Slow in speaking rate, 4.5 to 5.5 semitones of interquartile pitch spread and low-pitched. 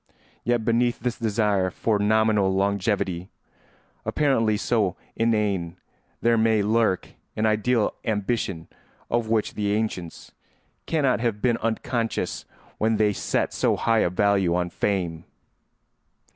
No: slow, 120 wpm; narrow, 2.6 semitones; low, 110 Hz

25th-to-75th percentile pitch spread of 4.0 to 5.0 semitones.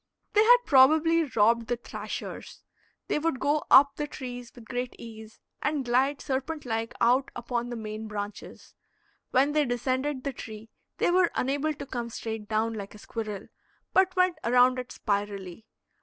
Yes: average, 4.4 semitones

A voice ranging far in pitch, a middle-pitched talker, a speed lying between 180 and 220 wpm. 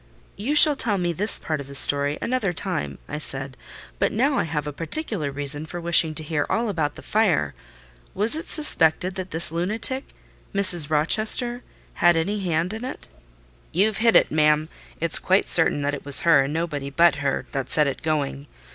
Yes: wide, 5.8 semitones; medium, 165 Hz; average, 190 wpm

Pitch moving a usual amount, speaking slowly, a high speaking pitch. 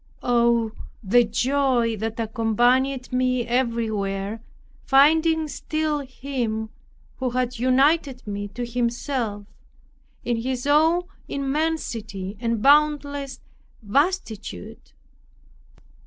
Yes: average, 3.9 semitones; slow, 85 wpm; high, 245 Hz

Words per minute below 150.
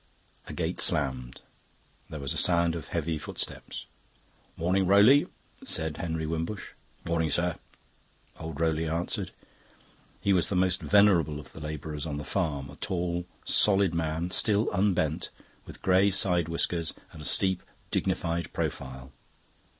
Yes: average, 140 wpm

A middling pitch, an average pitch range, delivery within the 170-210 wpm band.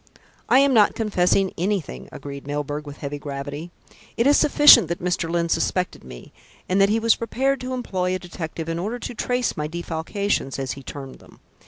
No: medium, 175 Hz; wide, 6.9 semitones; average, 195 wpm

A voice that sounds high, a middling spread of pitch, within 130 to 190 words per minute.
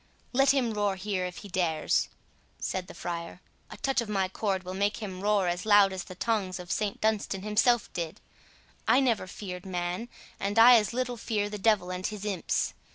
No: high, 200 Hz; average, 3.0 semitones; average, 200 wpm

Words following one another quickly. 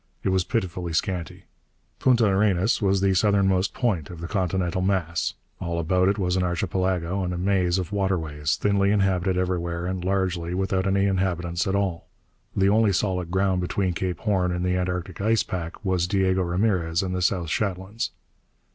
No: average, 175 wpm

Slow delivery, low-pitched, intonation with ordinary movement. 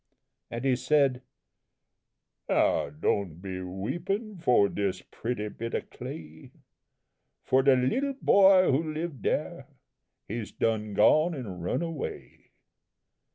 No: slow, 115 wpm; low, 125 Hz; wide, 8.2 semitones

